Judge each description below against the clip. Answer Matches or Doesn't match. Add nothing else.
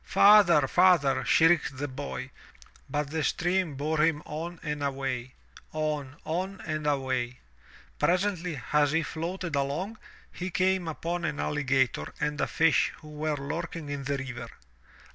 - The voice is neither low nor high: Matches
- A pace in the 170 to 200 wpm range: Doesn't match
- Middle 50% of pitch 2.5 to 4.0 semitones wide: Matches